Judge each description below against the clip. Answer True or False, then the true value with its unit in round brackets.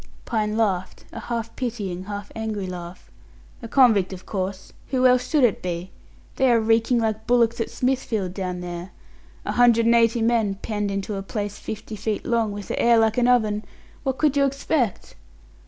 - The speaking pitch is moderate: False (220 Hz)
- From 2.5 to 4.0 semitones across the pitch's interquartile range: True (3.3 semitones)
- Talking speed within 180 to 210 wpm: True (185 wpm)